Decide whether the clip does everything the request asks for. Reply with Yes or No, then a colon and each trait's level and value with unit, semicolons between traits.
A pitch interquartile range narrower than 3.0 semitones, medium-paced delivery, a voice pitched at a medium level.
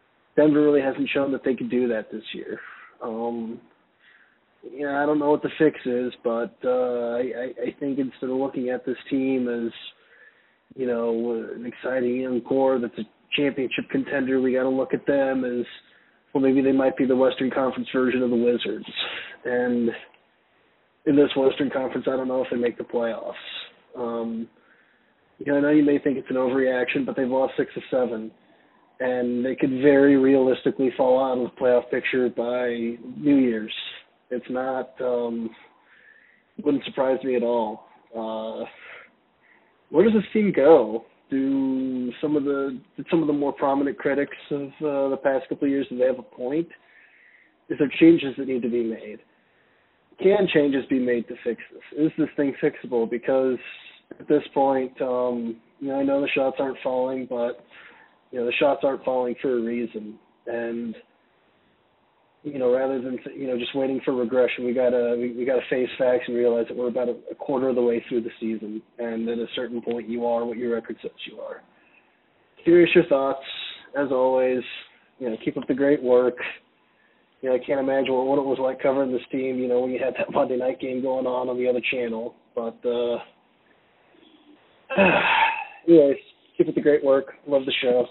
No: narrow, 2.4 semitones; average, 190 wpm; low, 130 Hz